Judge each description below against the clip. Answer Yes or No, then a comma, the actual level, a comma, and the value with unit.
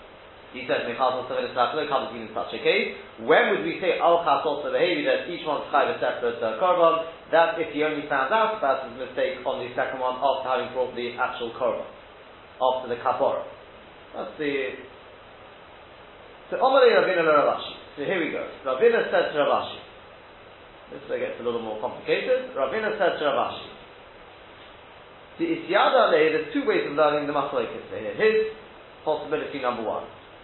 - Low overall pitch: No, medium, 180 Hz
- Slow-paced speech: No, average, 170 wpm